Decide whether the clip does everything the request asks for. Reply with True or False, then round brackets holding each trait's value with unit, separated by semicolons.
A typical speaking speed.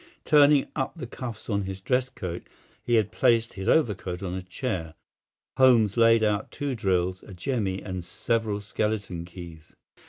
True (150 wpm)